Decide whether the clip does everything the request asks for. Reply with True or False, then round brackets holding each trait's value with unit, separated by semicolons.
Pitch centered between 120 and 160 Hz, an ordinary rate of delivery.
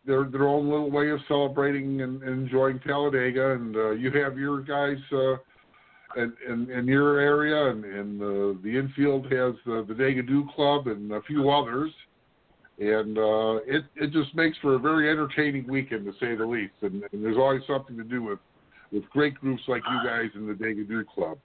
True (135 Hz; 195 wpm)